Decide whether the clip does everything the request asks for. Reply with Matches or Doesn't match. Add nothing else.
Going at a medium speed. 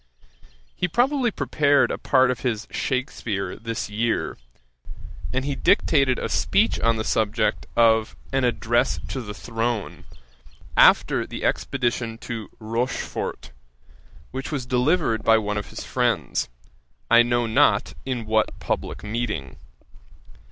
Doesn't match